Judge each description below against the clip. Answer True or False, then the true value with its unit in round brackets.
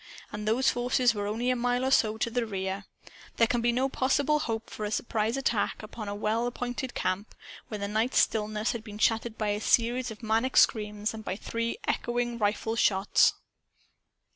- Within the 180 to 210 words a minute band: True (190 wpm)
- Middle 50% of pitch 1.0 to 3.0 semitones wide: True (2.4 semitones)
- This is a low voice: False (225 Hz)